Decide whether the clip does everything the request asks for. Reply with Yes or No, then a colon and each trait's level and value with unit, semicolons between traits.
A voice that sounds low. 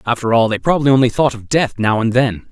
Yes: low, 120 Hz